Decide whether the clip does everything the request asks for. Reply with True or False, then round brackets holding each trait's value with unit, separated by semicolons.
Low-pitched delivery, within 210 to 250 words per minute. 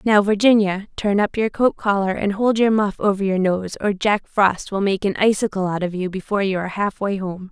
False (200 Hz; 230 wpm)